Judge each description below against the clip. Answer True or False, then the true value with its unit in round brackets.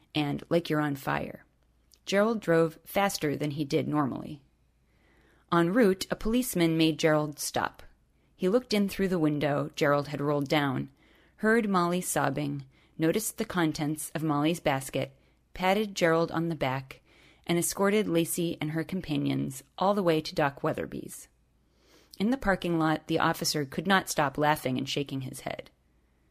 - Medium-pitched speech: True (160 Hz)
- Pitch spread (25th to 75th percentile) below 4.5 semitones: True (3.6 semitones)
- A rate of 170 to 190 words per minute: False (155 wpm)